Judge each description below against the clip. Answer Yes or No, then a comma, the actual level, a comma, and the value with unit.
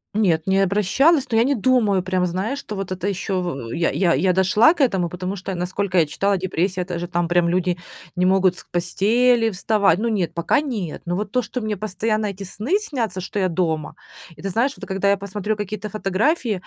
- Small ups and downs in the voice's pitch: No, average, 3.2 semitones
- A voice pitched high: Yes, high, 195 Hz